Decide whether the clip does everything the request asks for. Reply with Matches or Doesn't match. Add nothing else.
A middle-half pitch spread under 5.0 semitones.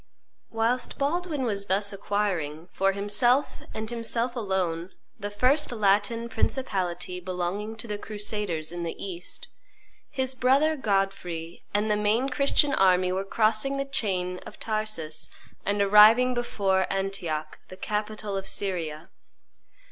Matches